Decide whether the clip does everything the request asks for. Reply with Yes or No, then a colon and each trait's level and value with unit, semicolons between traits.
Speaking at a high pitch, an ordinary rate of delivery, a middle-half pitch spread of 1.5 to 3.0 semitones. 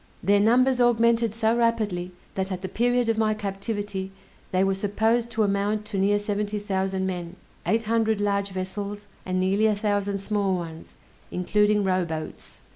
Yes: high, 205 Hz; average, 160 wpm; narrow, 2.5 semitones